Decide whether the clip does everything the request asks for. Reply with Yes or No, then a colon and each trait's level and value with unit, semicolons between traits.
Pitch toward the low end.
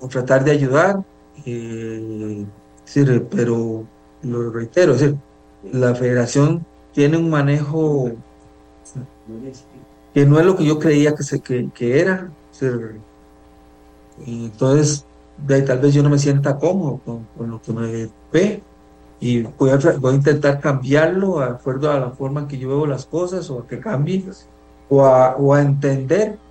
Yes: low, 130 Hz